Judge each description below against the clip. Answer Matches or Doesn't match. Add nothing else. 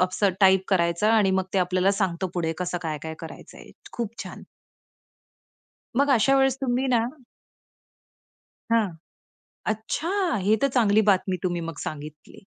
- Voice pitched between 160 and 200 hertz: Matches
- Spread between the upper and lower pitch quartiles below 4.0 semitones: Doesn't match